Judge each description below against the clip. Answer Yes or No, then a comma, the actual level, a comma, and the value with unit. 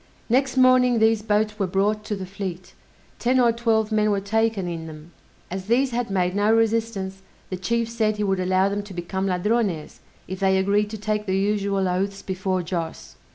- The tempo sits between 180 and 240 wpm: Yes, average, 195 wpm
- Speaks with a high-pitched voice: Yes, high, 205 Hz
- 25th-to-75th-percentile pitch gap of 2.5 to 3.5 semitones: Yes, average, 2.9 semitones